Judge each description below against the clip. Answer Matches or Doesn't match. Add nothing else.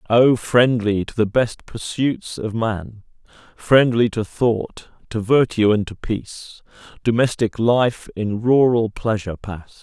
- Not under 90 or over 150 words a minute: Matches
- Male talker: Matches